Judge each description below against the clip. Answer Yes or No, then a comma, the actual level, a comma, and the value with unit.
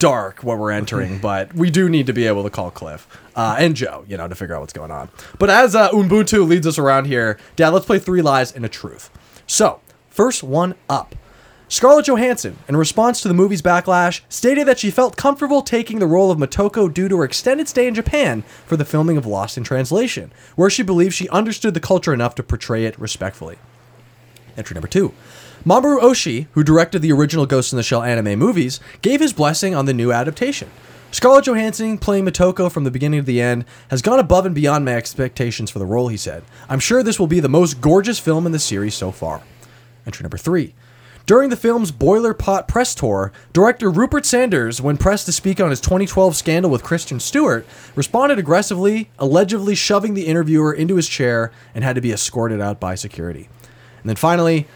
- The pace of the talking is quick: Yes, fast, 210 wpm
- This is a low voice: No, medium, 160 Hz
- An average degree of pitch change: No, wide, 8.5 semitones